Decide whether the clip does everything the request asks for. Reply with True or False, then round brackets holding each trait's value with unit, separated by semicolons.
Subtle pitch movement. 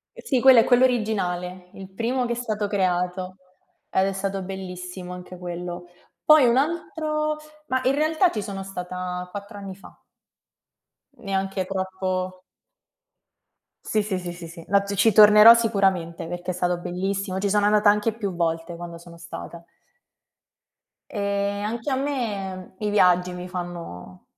False (3.0 semitones)